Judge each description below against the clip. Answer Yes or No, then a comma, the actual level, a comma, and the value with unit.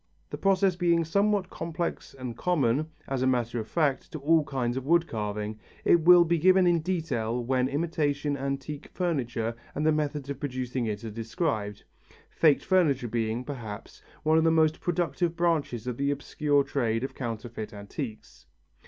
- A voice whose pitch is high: No, medium, 140 Hz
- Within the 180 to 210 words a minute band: No, average, 170 wpm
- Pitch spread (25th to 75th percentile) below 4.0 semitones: No, wide, 5.5 semitones